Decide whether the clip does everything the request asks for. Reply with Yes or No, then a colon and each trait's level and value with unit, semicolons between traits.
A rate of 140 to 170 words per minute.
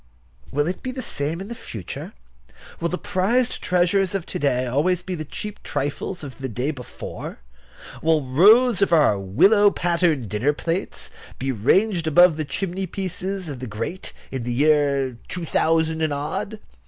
Yes: average, 165 wpm